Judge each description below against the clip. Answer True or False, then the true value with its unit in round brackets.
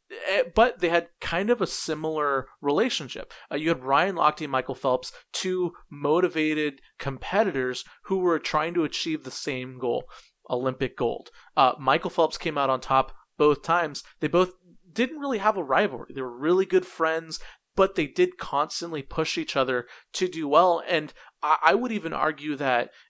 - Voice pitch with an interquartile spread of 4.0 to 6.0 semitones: True (4.9 semitones)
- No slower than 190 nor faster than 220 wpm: False (175 wpm)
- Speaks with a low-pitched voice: False (160 Hz)